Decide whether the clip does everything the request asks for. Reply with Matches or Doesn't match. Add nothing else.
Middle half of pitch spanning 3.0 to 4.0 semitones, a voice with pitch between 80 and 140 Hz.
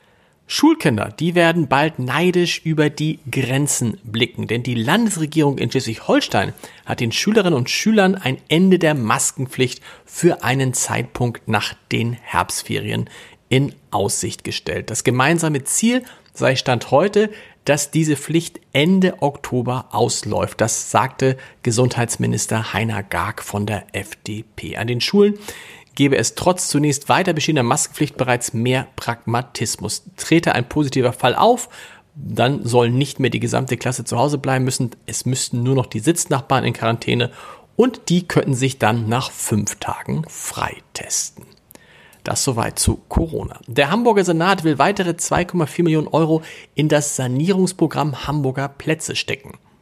Doesn't match